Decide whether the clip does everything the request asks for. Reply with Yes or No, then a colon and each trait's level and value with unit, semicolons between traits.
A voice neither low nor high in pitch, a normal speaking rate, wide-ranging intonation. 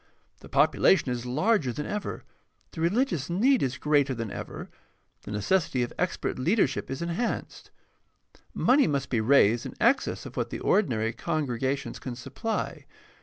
Yes: medium, 145 Hz; average, 150 wpm; wide, 7.4 semitones